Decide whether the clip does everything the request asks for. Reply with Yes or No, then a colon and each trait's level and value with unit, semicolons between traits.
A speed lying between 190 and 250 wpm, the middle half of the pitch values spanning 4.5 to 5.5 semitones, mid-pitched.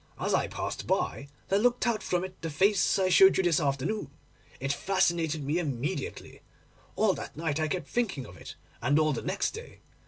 Yes: average, 195 wpm; average, 5.0 semitones; medium, 165 Hz